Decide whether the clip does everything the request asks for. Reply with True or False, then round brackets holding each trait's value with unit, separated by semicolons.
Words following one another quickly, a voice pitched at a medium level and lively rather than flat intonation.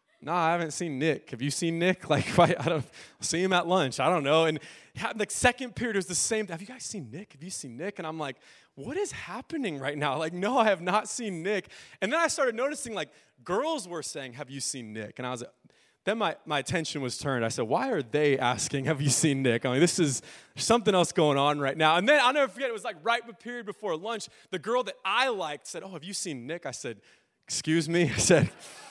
True (255 wpm; 170 Hz; 6.2 semitones)